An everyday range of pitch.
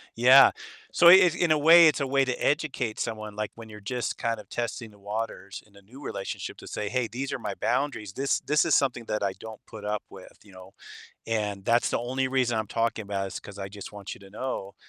Yes: average, 4.4 semitones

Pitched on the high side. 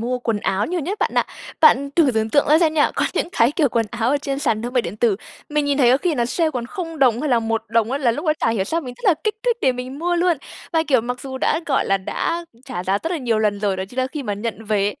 Yes: very high, 255 Hz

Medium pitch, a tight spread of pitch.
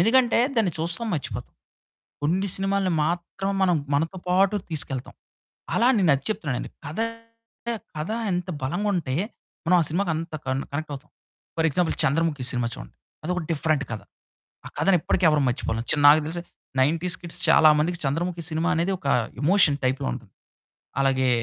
No: medium, 165 Hz; average, 4.2 semitones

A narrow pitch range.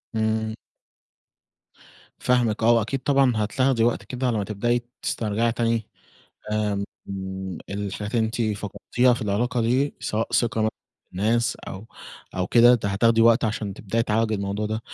Yes: narrow, 2.1 semitones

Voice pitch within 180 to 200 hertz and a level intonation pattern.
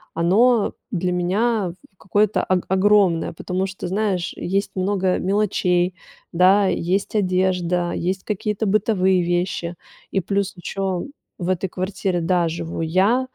Yes: medium, 185 Hz; narrow, 2.2 semitones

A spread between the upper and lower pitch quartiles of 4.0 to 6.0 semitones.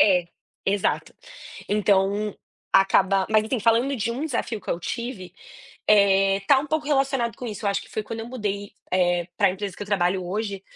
No: average, 3.3 semitones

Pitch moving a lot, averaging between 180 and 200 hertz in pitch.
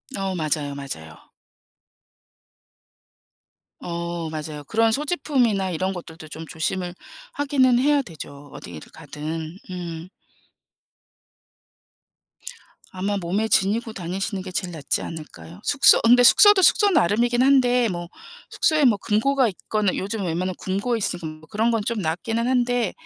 Yes: wide, 6.4 semitones; high, 190 Hz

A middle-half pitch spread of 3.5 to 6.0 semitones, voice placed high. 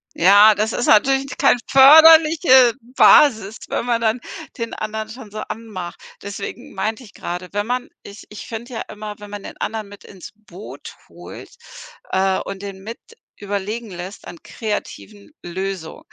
No: average, 2.9 semitones; high, 215 Hz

